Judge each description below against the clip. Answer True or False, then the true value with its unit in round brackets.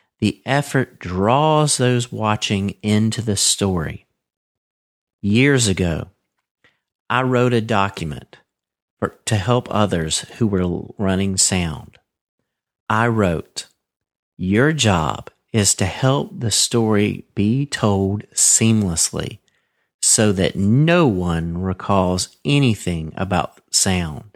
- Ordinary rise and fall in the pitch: True (4.0 semitones)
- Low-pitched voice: True (105 Hz)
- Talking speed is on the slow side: True (105 wpm)